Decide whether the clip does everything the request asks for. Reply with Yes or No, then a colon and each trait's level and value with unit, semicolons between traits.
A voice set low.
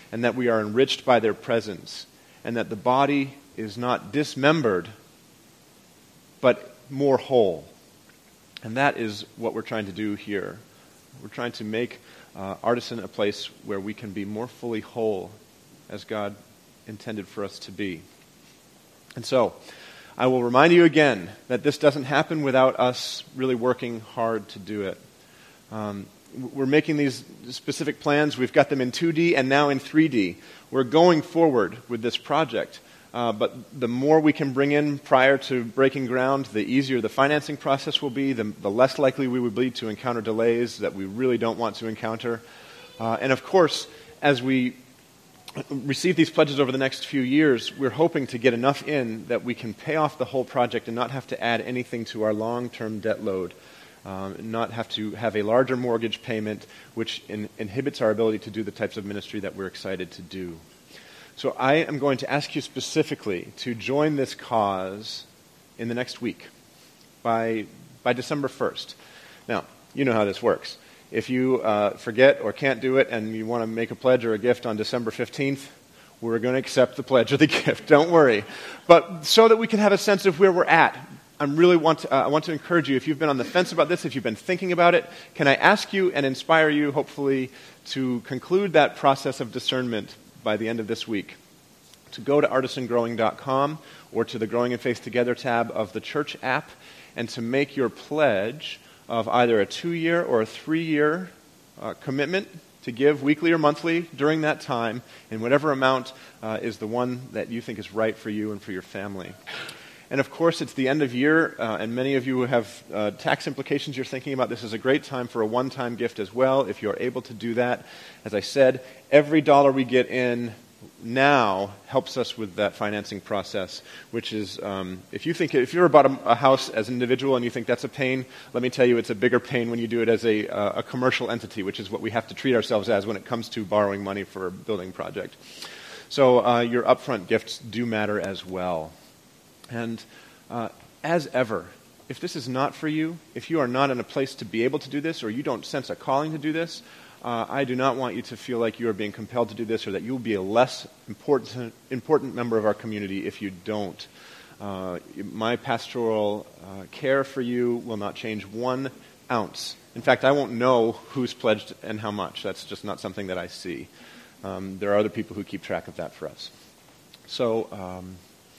Yes: low, 125 Hz